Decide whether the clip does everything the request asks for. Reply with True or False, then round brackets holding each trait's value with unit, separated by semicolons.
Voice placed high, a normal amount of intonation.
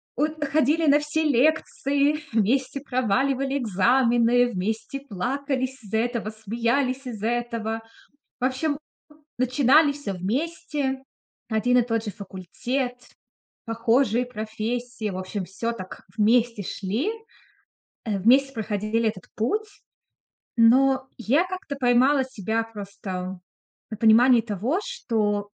True (240 Hz; 3.9 semitones)